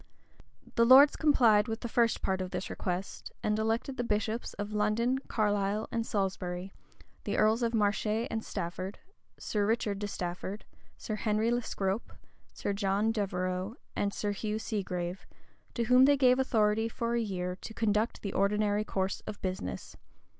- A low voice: No, high, 210 Hz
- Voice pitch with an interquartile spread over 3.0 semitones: No, average, 2.7 semitones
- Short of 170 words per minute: Yes, average, 160 wpm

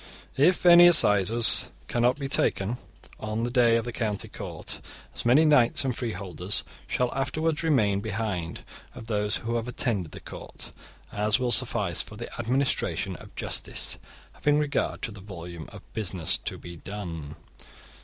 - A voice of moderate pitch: No, low, 115 Hz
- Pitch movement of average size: Yes, average, 4.5 semitones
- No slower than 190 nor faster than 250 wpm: No, average, 160 wpm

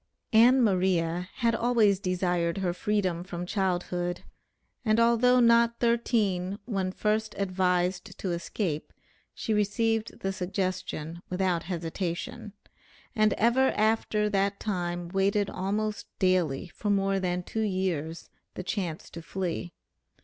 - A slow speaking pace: Yes, slow, 120 wpm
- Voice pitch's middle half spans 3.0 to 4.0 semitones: Yes, average, 3.3 semitones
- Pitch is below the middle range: No, high, 195 Hz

